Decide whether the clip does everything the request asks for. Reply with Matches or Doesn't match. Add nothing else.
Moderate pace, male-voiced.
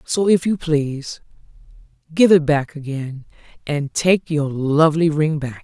Doesn't match